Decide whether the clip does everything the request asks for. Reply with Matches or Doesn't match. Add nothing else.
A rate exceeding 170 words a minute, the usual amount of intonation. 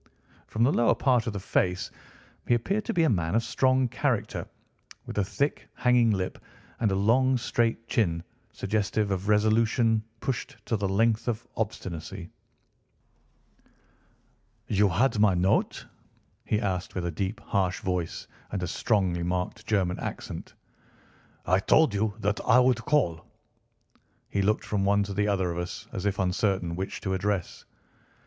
Doesn't match